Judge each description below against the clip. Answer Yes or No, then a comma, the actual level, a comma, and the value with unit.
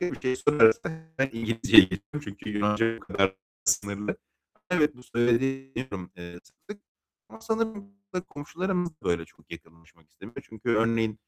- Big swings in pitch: Yes, wide, 6.5 semitones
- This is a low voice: Yes, low, 115 Hz